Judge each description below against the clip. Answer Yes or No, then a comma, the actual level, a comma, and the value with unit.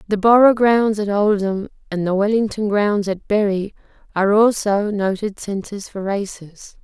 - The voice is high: Yes, high, 205 Hz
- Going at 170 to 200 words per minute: No, average, 150 wpm